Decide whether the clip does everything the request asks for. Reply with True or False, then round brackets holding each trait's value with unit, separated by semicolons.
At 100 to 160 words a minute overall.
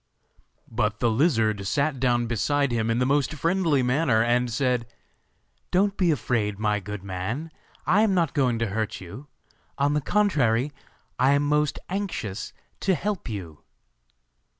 True (150 wpm)